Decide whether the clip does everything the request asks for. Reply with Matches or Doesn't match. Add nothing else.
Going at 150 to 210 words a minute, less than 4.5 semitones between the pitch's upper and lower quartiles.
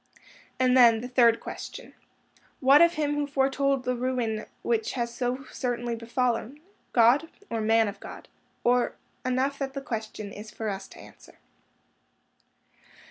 Doesn't match